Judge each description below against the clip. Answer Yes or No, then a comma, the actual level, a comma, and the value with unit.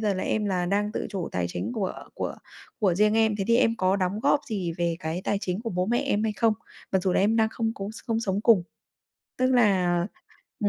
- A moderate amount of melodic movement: Yes, average, 3.3 semitones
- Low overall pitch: No, high, 205 Hz